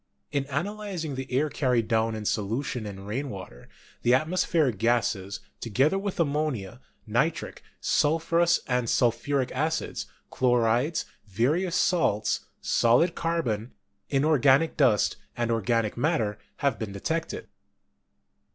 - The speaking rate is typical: No, slow, 120 wpm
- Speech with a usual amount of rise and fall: No, wide, 5.8 semitones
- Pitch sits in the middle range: No, low, 130 Hz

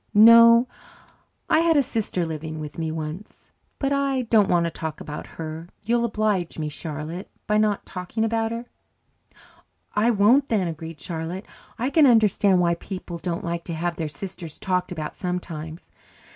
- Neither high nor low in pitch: Yes, medium, 180 Hz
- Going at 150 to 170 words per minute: Yes, average, 165 wpm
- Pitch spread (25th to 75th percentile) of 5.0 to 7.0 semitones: Yes, wide, 5.6 semitones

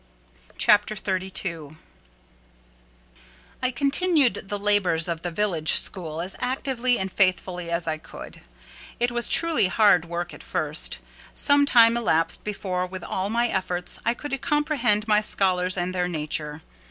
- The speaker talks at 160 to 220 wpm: No, average, 140 wpm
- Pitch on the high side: Yes, high, 195 Hz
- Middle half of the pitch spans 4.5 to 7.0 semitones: Yes, average, 5.2 semitones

